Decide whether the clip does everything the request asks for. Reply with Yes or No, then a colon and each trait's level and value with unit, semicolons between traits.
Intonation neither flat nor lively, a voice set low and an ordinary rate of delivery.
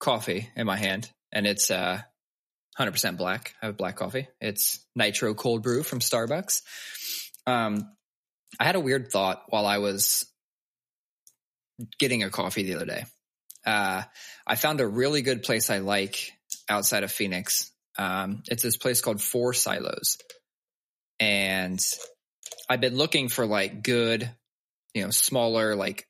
Yes: average, 4.1 semitones; low, 120 Hz; average, 150 wpm